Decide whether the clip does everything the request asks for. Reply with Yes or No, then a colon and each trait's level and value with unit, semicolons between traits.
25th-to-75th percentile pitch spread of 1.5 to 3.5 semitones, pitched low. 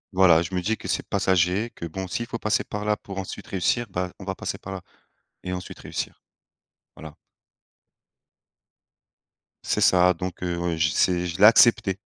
Yes: narrow, 2.4 semitones; very low, 95 Hz